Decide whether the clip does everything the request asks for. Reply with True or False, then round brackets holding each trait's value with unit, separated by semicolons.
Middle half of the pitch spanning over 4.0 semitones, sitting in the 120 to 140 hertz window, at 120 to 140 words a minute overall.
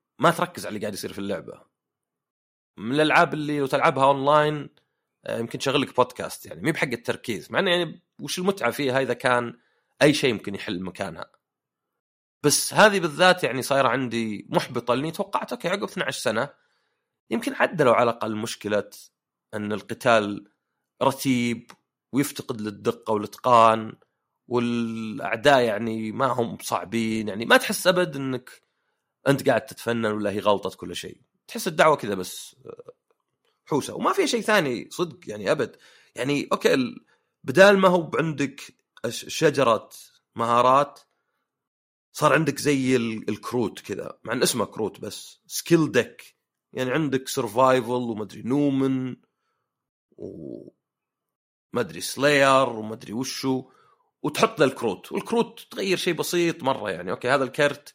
True (5.6 semitones; 135 Hz; 135 wpm)